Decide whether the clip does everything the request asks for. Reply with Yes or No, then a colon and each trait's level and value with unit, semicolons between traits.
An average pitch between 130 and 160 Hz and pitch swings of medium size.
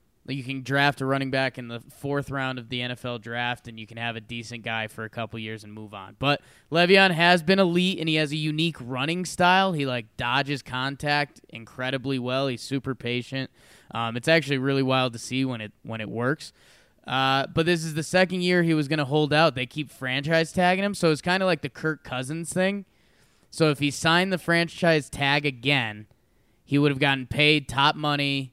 Yes: medium, 140 Hz; average, 4.3 semitones